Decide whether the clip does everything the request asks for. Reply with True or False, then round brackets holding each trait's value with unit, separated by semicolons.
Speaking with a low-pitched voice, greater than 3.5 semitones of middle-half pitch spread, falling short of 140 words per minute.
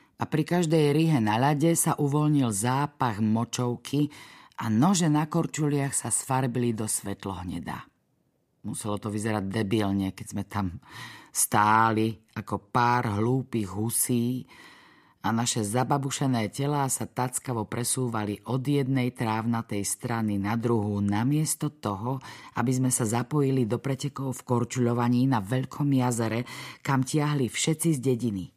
True (120 Hz; 3.9 semitones; 130 wpm)